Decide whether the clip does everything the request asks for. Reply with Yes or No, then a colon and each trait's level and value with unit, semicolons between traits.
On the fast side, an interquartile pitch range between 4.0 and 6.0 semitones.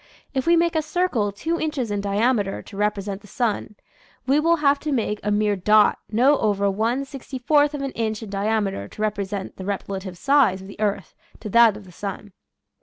Yes: fast, 210 wpm; average, 5.3 semitones